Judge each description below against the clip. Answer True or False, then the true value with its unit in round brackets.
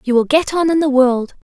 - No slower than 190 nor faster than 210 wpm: False (270 wpm)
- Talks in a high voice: True (275 Hz)